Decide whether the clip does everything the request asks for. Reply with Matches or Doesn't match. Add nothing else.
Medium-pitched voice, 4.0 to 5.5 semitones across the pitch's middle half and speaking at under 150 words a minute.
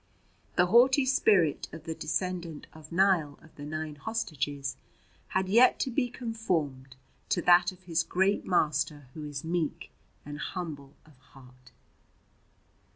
Matches